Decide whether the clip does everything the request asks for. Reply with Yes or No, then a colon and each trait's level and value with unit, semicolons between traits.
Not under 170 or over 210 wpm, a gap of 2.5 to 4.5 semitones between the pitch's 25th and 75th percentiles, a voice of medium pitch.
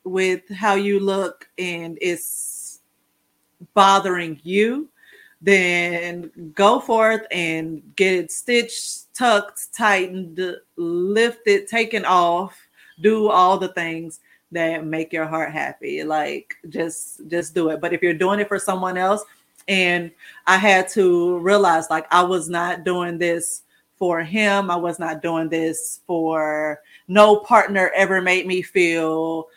No: slow, 135 wpm; average, 2.9 semitones; medium, 180 Hz